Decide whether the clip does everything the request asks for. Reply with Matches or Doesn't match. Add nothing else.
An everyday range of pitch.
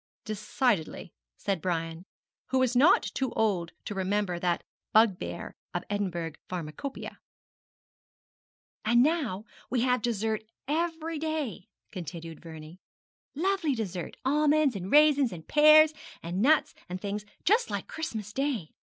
Doesn't match